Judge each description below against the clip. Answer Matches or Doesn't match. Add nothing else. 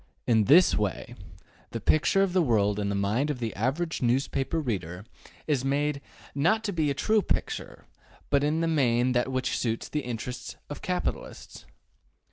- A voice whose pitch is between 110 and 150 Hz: Matches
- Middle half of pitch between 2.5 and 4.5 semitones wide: Doesn't match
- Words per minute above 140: Matches